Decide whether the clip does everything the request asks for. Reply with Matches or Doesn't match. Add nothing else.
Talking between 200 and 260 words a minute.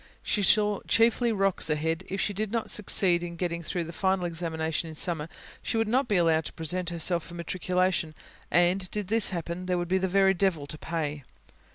Matches